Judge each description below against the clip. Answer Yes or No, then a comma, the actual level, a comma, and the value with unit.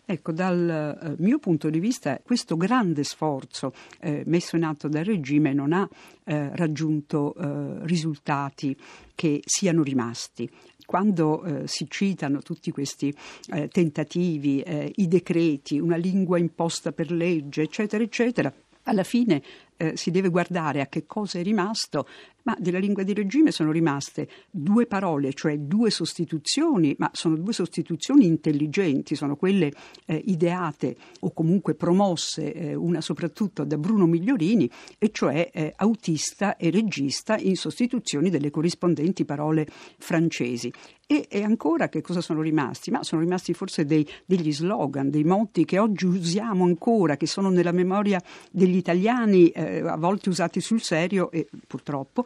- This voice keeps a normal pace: Yes, average, 150 wpm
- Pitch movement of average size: Yes, average, 3.8 semitones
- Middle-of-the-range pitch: Yes, medium, 170 Hz